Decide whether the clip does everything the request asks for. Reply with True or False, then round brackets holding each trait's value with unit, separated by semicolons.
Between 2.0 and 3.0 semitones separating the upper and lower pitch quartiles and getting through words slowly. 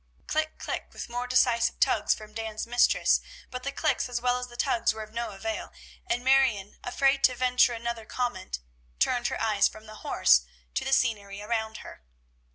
False (2.5 semitones; 185 wpm)